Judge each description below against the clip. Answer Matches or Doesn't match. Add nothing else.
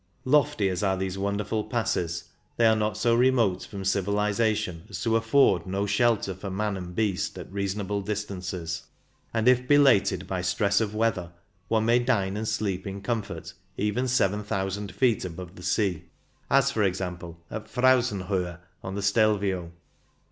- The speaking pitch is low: Matches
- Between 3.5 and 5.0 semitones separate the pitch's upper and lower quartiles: Doesn't match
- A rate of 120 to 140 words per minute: Doesn't match